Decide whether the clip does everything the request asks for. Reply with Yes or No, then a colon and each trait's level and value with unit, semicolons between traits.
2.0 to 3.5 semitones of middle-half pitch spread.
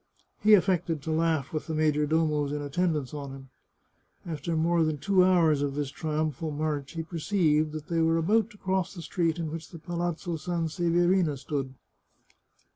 Yes: narrow, 2.5 semitones